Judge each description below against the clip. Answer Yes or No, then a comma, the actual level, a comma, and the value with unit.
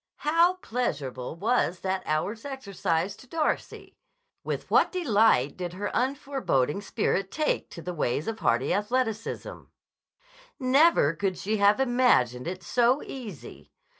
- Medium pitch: No, high, 210 Hz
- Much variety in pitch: Yes, wide, 6.8 semitones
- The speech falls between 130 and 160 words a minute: Yes, slow, 135 wpm